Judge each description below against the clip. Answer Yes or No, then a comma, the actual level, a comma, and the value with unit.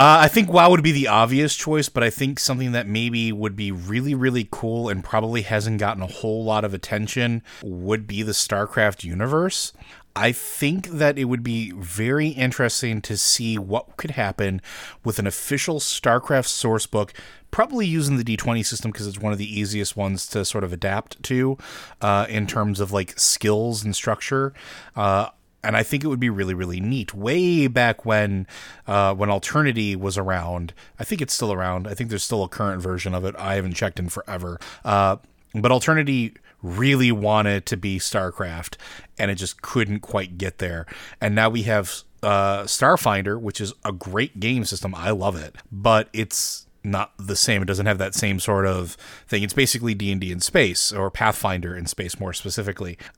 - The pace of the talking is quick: No, average, 190 wpm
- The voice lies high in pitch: No, low, 105 Hz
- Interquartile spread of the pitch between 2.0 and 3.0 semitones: No, average, 3.6 semitones